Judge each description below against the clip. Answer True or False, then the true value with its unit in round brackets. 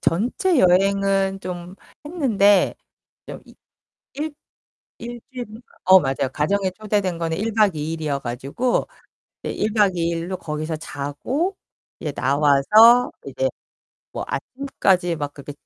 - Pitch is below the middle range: False (190 Hz)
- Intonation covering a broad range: True (6.3 semitones)